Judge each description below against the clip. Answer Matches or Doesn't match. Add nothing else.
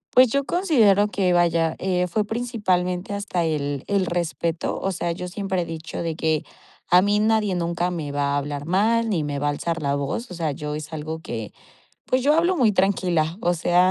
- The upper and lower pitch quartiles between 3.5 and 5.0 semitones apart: Matches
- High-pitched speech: Doesn't match